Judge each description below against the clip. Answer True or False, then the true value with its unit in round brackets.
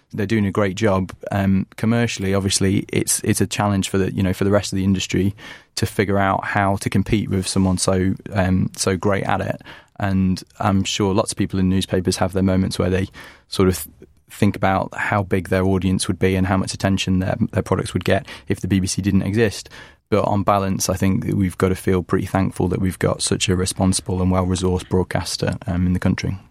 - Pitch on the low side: True (95 Hz)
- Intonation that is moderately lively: False (1.3 semitones)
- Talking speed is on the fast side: True (225 wpm)